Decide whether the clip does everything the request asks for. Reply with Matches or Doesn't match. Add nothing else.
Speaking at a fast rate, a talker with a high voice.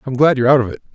Doesn't match